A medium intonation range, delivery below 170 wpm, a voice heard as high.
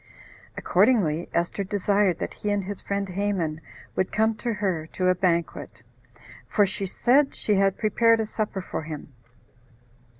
Yes: average, 3.1 semitones; average, 155 wpm; high, 195 Hz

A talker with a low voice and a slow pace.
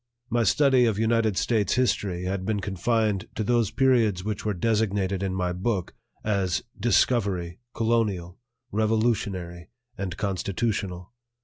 Yes: low, 105 Hz; slow, 125 wpm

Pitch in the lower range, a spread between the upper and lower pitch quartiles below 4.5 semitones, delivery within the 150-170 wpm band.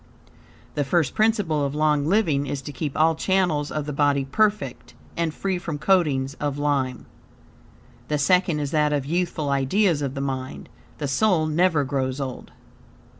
No: medium, 150 Hz; average, 3.6 semitones; average, 165 wpm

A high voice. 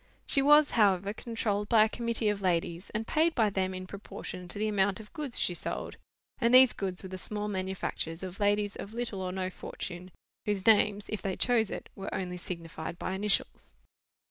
Yes: high, 200 Hz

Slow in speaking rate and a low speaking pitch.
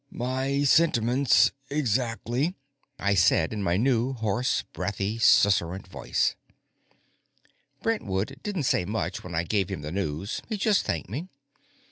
Yes: slow, 130 wpm; low, 110 Hz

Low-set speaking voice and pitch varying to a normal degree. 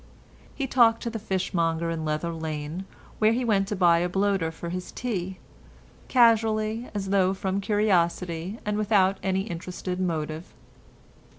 No: high, 190 Hz; average, 3.9 semitones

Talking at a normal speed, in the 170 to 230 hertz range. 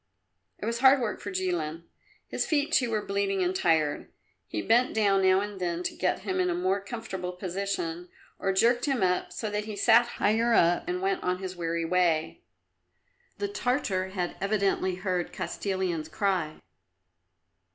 Yes: average, 170 wpm; high, 190 Hz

